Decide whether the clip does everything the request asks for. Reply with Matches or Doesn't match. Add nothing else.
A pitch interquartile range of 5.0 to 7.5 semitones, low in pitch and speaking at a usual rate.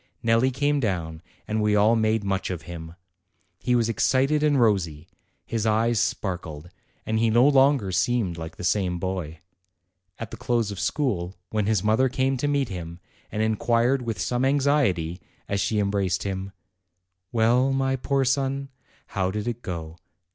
Matches